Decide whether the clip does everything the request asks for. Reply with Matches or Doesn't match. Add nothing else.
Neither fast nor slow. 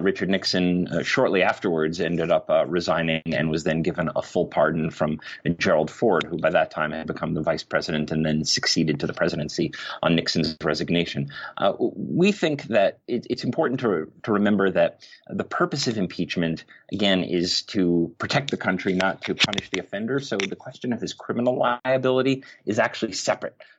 Matches